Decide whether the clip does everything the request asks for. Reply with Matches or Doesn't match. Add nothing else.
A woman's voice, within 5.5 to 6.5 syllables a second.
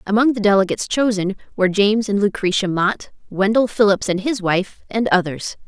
Matches